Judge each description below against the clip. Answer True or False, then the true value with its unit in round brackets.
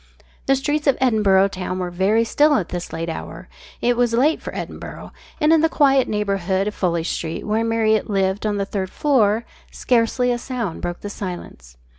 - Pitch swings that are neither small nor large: True (4.7 semitones)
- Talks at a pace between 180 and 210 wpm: True (190 wpm)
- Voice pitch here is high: True (210 Hz)